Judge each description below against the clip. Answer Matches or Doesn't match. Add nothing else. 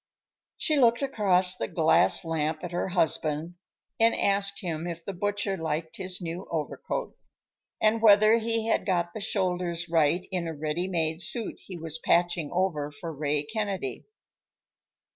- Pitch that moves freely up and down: Doesn't match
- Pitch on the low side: Doesn't match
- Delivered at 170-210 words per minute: Doesn't match